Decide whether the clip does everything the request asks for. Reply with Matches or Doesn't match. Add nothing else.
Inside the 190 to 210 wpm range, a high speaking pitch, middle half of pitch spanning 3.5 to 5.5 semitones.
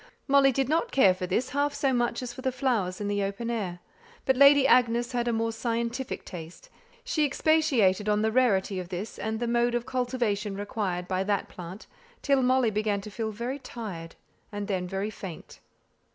Matches